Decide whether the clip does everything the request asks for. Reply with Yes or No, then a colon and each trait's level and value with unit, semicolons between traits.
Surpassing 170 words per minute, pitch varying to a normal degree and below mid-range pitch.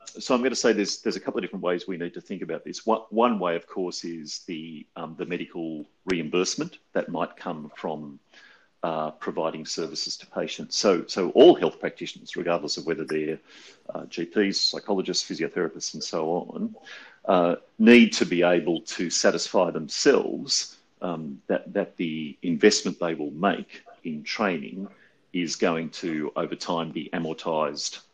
No: average, 165 wpm; average, 3.7 semitones; very low, 85 Hz